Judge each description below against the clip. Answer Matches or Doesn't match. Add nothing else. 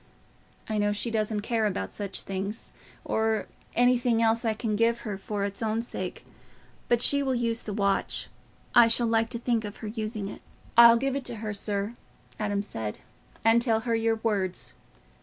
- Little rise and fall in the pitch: Matches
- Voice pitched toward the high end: Matches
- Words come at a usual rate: Matches